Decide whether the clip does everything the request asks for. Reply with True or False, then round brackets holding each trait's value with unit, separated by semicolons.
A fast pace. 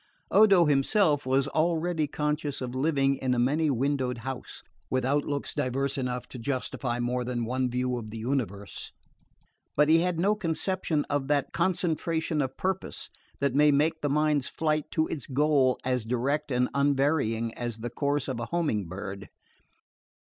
False (160 wpm)